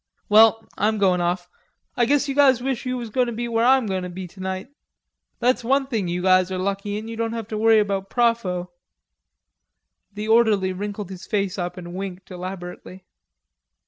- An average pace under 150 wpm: No, average, 185 wpm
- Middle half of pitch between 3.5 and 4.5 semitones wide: Yes, average, 3.9 semitones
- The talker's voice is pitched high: Yes, high, 205 Hz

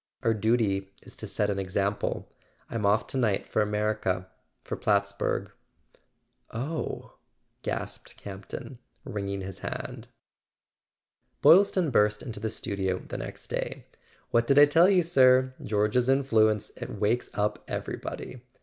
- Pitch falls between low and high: No, low, 110 Hz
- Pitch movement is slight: No, average, 4.2 semitones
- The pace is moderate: No, slow, 130 wpm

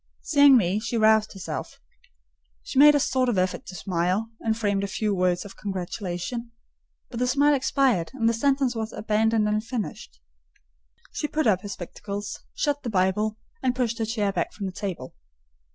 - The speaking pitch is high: Yes, high, 215 Hz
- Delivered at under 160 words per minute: No, average, 175 wpm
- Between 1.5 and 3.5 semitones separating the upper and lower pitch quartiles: No, average, 4.3 semitones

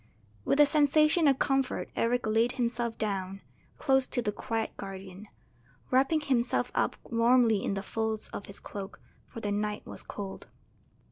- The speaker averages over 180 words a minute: No, average, 155 wpm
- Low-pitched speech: No, high, 230 Hz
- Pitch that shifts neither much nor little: Yes, average, 4.4 semitones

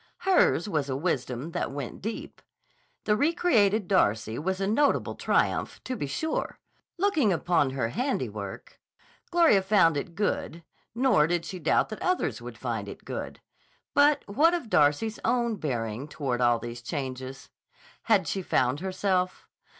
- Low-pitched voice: No, medium, 185 Hz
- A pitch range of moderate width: No, wide, 8.5 semitones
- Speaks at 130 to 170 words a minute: Yes, average, 150 wpm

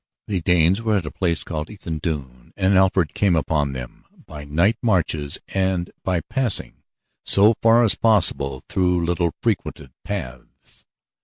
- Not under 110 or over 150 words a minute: Yes, average, 145 wpm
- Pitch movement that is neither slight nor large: Yes, average, 4.5 semitones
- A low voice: Yes, very low, 90 Hz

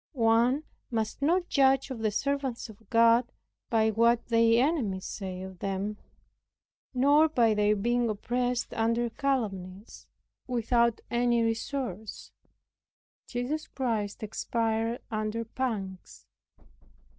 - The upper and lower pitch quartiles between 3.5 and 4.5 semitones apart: No, average, 2.7 semitones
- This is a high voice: Yes, high, 230 Hz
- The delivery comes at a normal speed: No, slow, 110 wpm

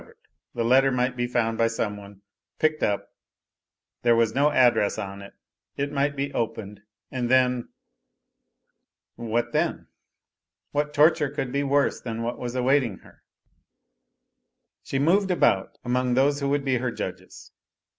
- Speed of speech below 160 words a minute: Yes, average, 150 wpm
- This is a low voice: Yes, low, 125 Hz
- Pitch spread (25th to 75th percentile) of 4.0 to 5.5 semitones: No, average, 3.4 semitones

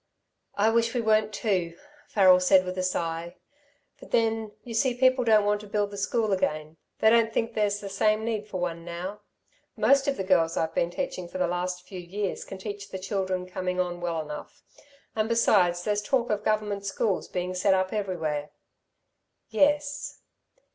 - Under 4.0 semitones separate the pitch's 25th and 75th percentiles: Yes, average, 3.3 semitones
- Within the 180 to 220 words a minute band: Yes, average, 185 wpm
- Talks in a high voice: Yes, high, 200 Hz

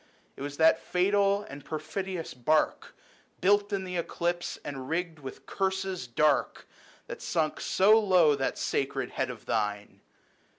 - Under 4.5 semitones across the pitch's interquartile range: No, average, 4.8 semitones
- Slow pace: No, average, 145 wpm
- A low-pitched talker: No, medium, 170 Hz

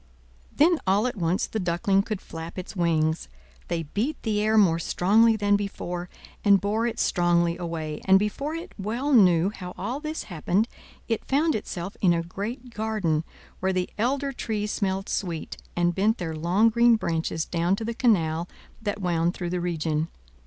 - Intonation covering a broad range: No, average, 4.3 semitones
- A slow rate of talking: No, average, 175 wpm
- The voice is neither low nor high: No, high, 195 Hz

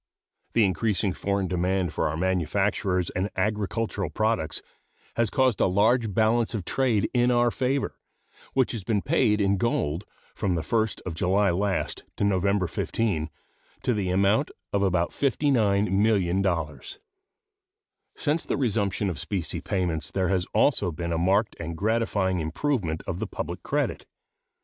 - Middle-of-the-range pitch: No, low, 100 Hz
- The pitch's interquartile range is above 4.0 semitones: No, average, 3.7 semitones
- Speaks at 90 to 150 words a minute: Yes, average, 145 wpm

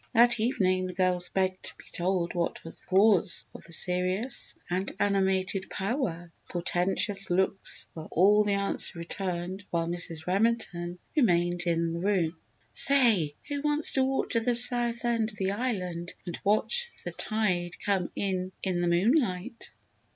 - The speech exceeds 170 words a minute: No, average, 160 wpm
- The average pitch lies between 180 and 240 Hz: Yes, high, 190 Hz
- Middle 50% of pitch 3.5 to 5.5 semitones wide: Yes, average, 4.0 semitones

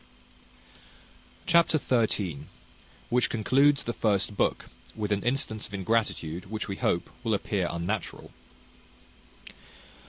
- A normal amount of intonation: Yes, average, 3.4 semitones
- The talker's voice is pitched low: Yes, low, 105 Hz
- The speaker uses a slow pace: Yes, slow, 105 wpm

